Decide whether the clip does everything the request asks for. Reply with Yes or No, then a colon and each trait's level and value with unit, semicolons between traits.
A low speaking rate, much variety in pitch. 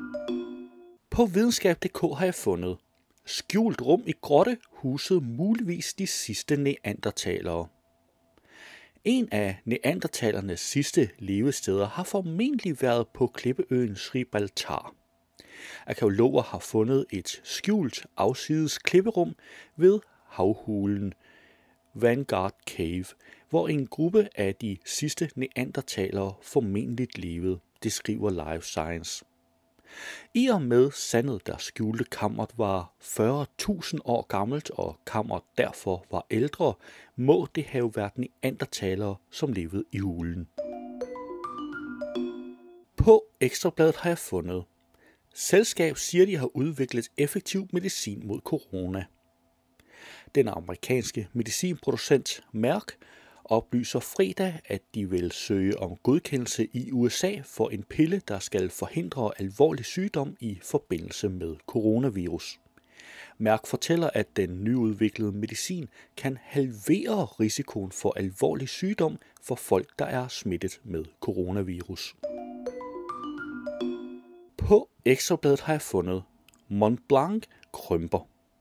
Yes: slow, 110 wpm; wide, 8.5 semitones